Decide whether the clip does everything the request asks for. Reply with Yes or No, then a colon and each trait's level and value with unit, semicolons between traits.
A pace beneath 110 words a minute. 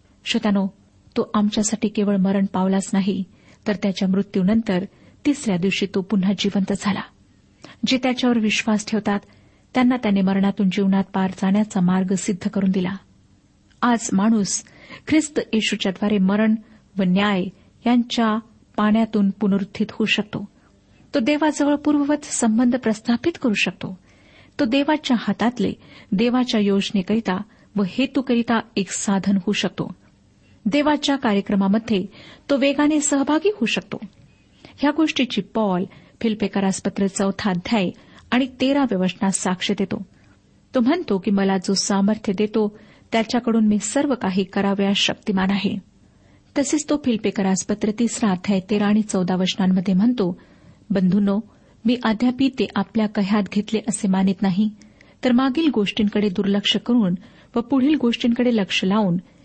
No: average, 120 wpm